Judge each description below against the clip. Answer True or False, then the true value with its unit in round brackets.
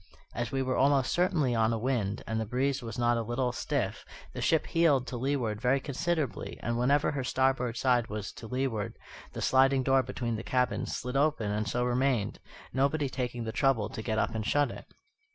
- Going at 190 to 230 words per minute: True (205 wpm)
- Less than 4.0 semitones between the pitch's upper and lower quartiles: True (2.9 semitones)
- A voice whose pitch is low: True (125 Hz)